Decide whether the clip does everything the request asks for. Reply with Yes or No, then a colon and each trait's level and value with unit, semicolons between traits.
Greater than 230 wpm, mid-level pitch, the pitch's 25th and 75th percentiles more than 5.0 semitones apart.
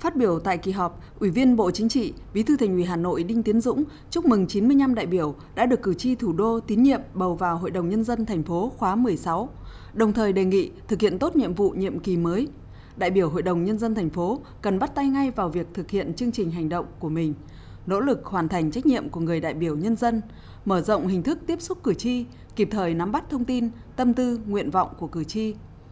No: fast, 250 wpm; high, 210 Hz; wide, 5.4 semitones